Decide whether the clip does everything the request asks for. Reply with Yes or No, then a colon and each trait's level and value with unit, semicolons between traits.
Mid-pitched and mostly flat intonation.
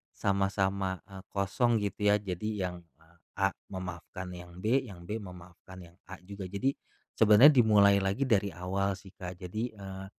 No: very low, 95 Hz; narrow, 2.1 semitones